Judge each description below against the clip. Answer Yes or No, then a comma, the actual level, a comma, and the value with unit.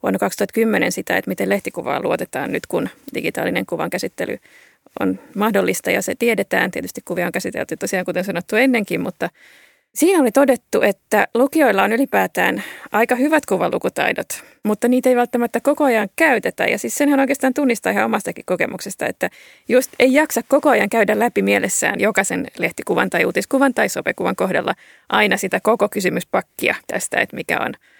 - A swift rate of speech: Yes, fast, 160 wpm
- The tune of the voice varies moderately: Yes, average, 4.6 semitones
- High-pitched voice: Yes, high, 240 Hz